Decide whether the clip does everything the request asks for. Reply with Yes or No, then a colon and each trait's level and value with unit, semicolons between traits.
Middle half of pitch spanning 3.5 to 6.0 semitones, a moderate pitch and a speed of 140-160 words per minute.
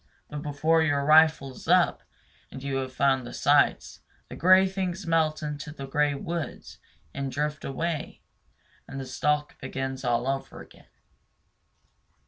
No: average, 2.8 semitones; medium, 145 Hz; average, 145 wpm